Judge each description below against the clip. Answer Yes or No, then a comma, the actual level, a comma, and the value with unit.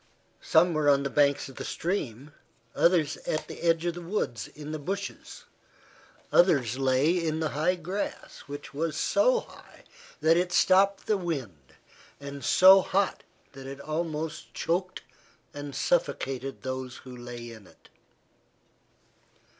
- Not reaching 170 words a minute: Yes, average, 145 wpm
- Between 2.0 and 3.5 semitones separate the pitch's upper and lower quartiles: No, average, 4.5 semitones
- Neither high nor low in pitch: Yes, medium, 155 Hz